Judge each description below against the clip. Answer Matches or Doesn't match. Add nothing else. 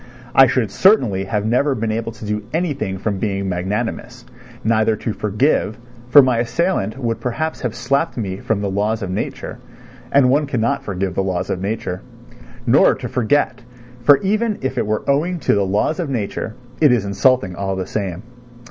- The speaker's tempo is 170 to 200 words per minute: Matches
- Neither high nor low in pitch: Doesn't match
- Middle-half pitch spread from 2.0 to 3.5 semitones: Doesn't match